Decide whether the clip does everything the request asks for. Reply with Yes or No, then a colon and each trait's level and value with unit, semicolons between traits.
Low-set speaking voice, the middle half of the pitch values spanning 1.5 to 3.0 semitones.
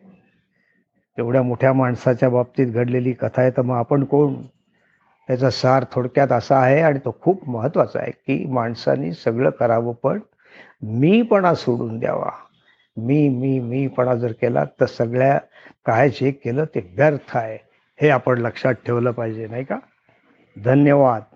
Yes: low, 130 Hz; narrow, 2.4 semitones